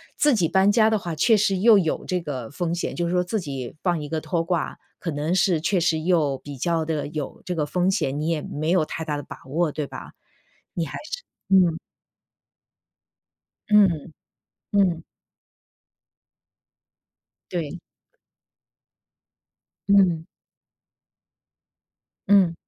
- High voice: No, medium, 170 Hz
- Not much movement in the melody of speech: No, average, 3.3 semitones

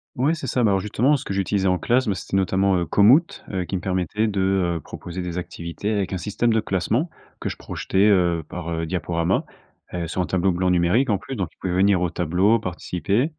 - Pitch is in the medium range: No, very low, 95 Hz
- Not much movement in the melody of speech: No, average, 3.2 semitones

